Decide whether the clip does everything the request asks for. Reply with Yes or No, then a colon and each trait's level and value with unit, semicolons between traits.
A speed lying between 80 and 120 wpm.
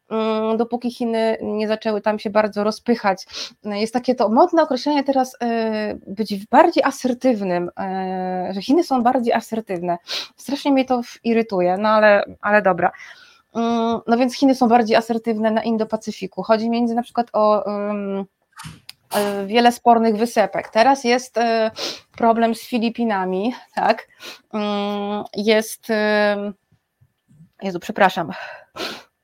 Yes: average, 115 wpm